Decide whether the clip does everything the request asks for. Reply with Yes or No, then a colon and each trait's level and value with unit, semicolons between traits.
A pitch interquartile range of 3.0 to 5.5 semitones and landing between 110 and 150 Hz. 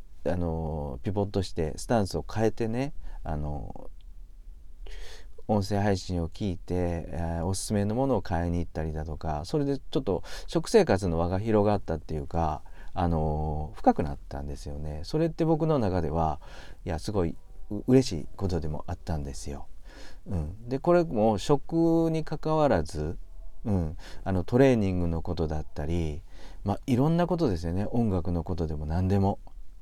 No: average, 5.2 semitones; very low, 85 Hz